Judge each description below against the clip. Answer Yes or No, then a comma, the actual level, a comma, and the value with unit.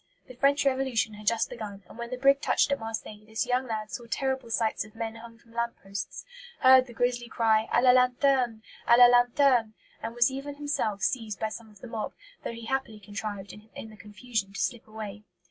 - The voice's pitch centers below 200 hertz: No, high, 230 Hz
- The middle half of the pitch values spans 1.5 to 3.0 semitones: Yes, average, 2.7 semitones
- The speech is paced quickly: Yes, fast, 215 wpm